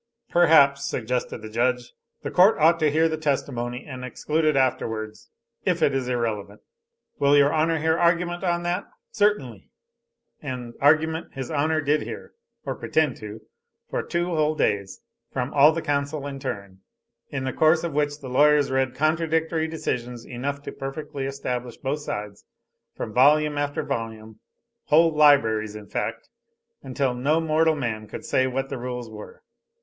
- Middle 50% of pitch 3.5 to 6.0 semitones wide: Yes, average, 4.0 semitones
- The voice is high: No, medium, 140 Hz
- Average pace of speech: Yes, average, 160 wpm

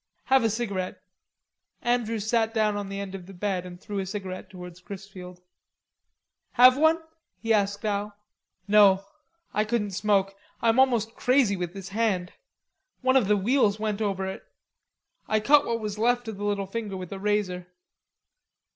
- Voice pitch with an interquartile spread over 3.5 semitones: No, average, 2.8 semitones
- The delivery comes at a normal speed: Yes, average, 170 wpm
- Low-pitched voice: No, high, 205 Hz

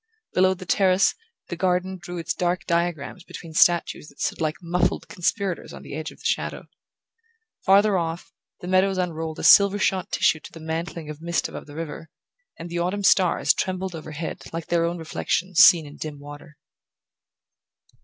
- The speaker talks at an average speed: Yes, average, 175 wpm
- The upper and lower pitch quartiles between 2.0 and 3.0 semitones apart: Yes, narrow, 2.5 semitones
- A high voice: No, medium, 170 Hz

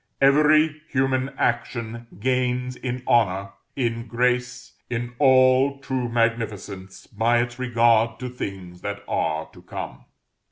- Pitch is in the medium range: No, low, 120 Hz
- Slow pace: Yes, slow, 120 wpm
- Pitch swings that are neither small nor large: No, narrow, 2.2 semitones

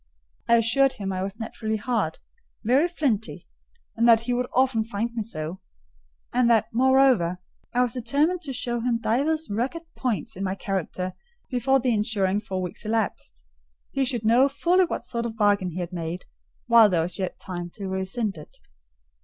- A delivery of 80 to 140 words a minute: No, average, 180 wpm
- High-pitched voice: Yes, high, 225 Hz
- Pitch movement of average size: Yes, average, 4.5 semitones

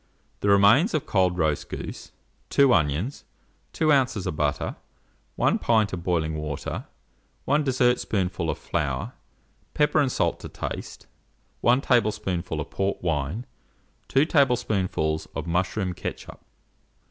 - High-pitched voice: No, low, 100 Hz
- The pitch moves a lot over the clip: Yes, wide, 7.2 semitones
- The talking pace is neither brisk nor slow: No, slow, 125 wpm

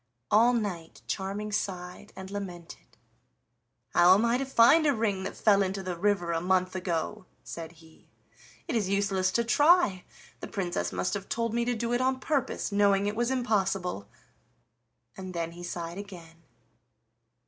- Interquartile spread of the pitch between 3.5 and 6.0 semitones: Yes, average, 4.2 semitones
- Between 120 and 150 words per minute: No, average, 165 wpm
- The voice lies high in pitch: Yes, high, 195 Hz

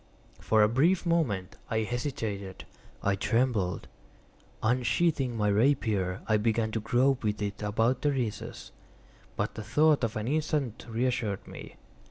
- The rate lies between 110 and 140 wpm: Yes, slow, 135 wpm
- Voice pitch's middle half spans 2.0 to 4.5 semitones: Yes, average, 3.9 semitones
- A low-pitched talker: Yes, low, 115 Hz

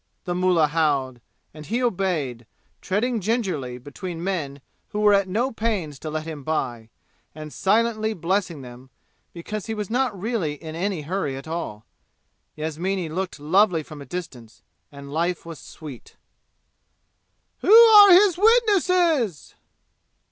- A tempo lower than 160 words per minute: Yes, average, 140 wpm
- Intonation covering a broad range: Yes, wide, 6.2 semitones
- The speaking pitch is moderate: Yes, medium, 175 Hz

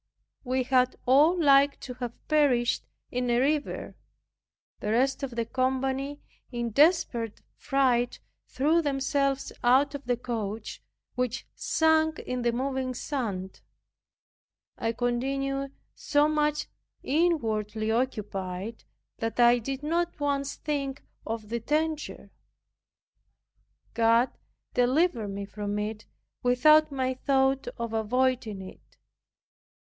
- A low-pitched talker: No, very high, 255 Hz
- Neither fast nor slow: No, slow, 110 wpm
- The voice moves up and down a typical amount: Yes, average, 3.4 semitones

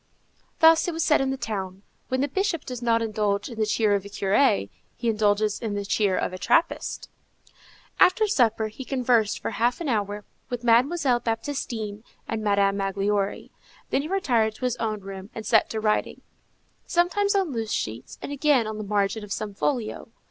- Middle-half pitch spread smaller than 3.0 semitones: No, average, 4.6 semitones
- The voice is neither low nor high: No, high, 225 Hz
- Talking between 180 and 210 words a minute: Yes, average, 190 wpm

